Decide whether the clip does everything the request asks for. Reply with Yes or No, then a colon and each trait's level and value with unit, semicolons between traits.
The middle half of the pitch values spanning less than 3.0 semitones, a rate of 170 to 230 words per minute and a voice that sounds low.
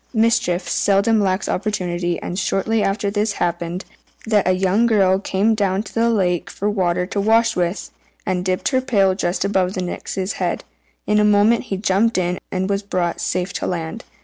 No: narrow, 2.6 semitones; average, 190 wpm; high, 195 Hz